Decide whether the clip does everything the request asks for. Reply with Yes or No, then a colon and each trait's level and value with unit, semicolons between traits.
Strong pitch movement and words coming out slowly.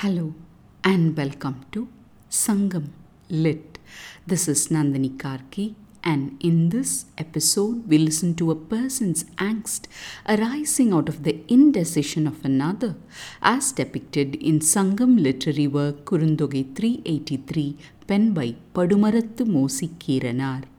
Yes: wide, 6.2 semitones; slow, 125 wpm